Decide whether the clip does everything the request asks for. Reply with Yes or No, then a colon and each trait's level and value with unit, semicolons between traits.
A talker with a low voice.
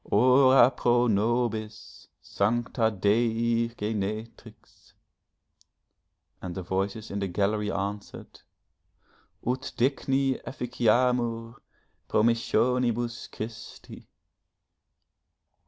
Yes: low, 115 Hz